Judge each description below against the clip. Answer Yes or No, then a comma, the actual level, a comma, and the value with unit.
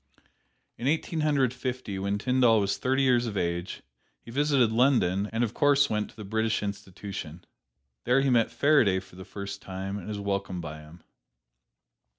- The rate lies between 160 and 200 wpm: Yes, average, 170 wpm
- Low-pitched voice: Yes, low, 105 Hz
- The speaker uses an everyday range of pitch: Yes, average, 4.7 semitones